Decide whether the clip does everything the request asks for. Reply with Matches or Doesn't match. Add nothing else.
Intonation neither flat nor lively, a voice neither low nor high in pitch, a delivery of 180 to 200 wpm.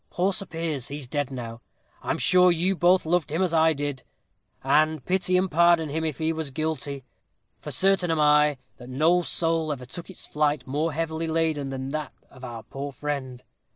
Matches